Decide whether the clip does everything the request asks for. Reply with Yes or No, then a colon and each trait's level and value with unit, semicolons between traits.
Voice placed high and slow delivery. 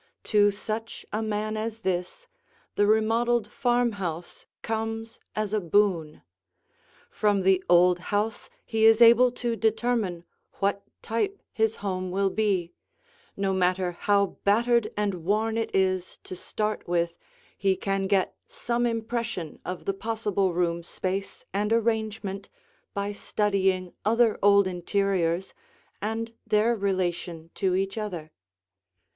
Yes: high, 205 Hz; slow, 130 wpm